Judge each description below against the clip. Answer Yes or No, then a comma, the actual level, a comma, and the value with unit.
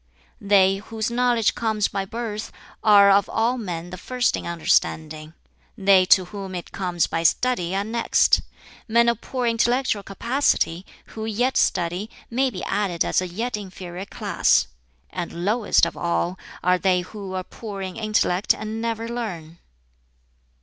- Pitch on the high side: Yes, high, 200 Hz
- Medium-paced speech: Yes, average, 155 wpm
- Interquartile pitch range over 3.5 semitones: Yes, average, 3.9 semitones